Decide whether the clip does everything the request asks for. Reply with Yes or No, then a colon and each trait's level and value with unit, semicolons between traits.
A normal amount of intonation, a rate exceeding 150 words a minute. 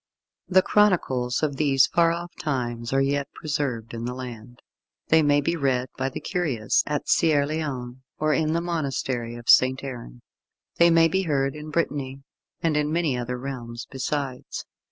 Yes: average, 3.9 semitones; average, 165 wpm